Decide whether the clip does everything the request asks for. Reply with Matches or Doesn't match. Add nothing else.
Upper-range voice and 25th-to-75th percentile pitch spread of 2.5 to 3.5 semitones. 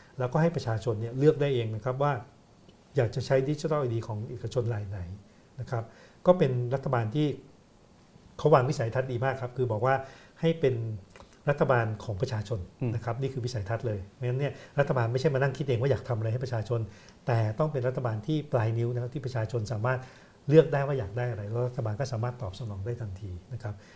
Doesn't match